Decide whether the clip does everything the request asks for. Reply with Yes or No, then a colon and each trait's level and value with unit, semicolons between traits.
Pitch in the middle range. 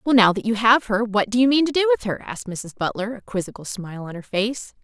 No: high, 225 Hz